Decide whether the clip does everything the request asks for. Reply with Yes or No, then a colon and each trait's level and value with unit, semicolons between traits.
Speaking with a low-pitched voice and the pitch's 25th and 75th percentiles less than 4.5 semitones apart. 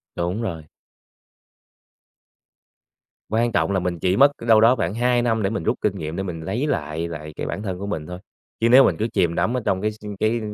No: low, 100 Hz; average, 5.1 semitones